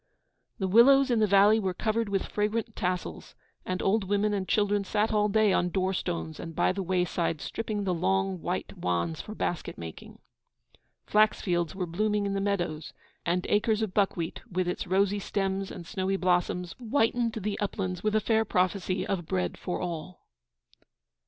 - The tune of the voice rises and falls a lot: No, average, 2.9 semitones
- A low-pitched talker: No, high, 195 Hz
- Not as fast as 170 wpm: No, average, 180 wpm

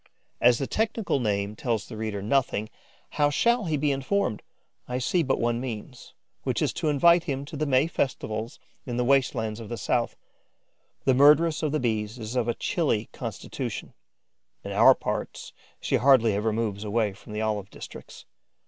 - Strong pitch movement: No, average, 4.7 semitones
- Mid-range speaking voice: No, low, 125 Hz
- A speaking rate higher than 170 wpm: Yes, average, 180 wpm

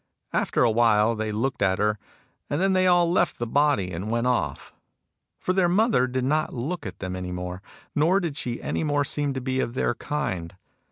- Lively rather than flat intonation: Yes, wide, 6.2 semitones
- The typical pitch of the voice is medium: No, low, 125 Hz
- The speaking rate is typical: No, fast, 210 wpm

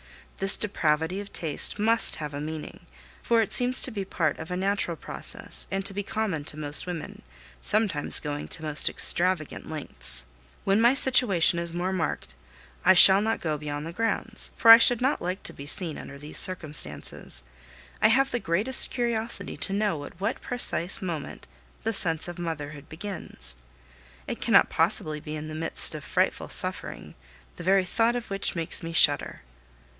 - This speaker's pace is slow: No, average, 180 wpm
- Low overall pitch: No, medium, 180 Hz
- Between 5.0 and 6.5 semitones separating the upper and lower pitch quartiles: Yes, wide, 5.4 semitones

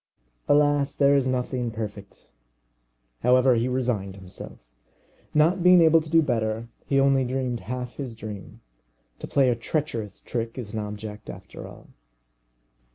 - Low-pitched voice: Yes, low, 125 Hz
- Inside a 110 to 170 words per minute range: Yes, average, 145 wpm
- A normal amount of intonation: Yes, average, 4.1 semitones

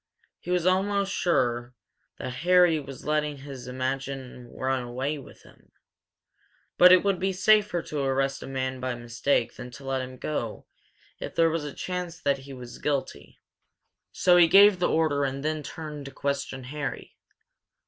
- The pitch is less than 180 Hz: Yes, medium, 140 Hz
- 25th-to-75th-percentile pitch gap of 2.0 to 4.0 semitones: No, average, 4.6 semitones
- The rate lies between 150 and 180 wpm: Yes, average, 170 wpm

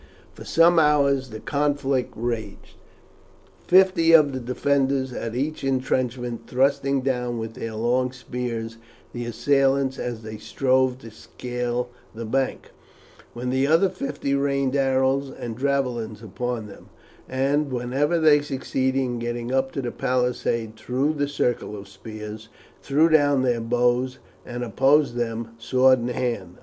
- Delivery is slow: No, average, 145 wpm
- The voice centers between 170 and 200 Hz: No, low, 130 Hz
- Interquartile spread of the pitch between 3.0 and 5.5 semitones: No, narrow, 2.6 semitones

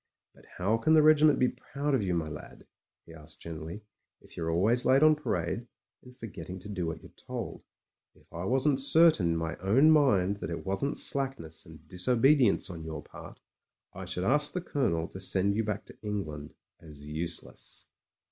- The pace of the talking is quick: No, average, 185 wpm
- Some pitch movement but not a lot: No, wide, 8.3 semitones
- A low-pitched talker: Yes, low, 100 Hz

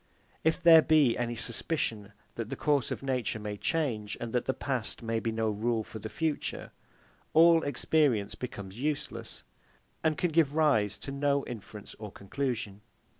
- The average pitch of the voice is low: Yes, low, 120 Hz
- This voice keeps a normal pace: Yes, average, 165 wpm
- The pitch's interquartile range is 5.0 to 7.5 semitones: Yes, wide, 5.4 semitones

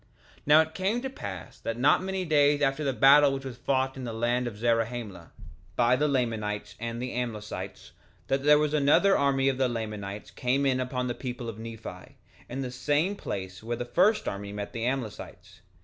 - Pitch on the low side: Yes, low, 125 Hz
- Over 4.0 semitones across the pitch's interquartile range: No, average, 3.7 semitones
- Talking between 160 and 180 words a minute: No, average, 200 wpm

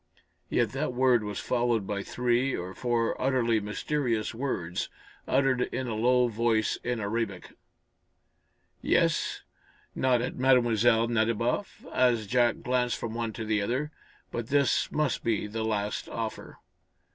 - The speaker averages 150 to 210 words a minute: No, slow, 135 wpm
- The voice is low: Yes, low, 120 Hz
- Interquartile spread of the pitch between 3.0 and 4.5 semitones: No, narrow, 2.5 semitones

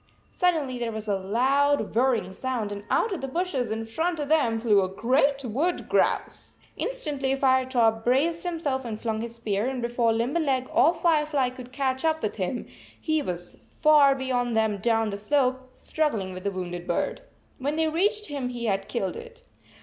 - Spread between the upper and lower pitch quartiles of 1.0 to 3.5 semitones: No, average, 5.0 semitones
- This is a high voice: Yes, very high, 255 Hz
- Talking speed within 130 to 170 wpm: No, average, 185 wpm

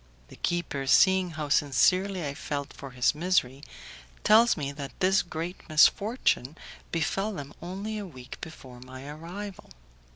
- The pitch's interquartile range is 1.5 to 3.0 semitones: No, average, 5.1 semitones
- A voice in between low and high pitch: Yes, medium, 160 Hz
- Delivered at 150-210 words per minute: No, average, 140 wpm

